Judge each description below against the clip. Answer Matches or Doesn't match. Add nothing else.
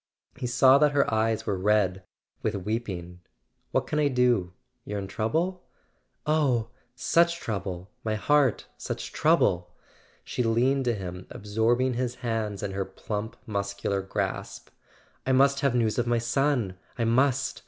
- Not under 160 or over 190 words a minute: Doesn't match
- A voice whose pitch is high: Doesn't match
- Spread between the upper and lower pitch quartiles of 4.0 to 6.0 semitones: Matches